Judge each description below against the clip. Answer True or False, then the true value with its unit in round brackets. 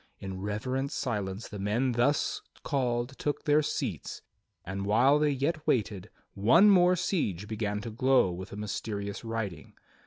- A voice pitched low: True (115 Hz)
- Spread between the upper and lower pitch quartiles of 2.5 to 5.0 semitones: False (5.5 semitones)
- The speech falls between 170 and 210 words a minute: False (150 wpm)